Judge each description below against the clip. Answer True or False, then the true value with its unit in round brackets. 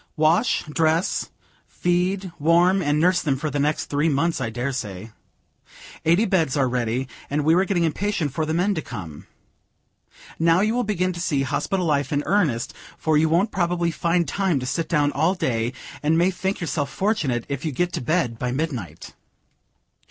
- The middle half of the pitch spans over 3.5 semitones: True (4.3 semitones)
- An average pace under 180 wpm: False (185 wpm)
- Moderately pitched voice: True (160 Hz)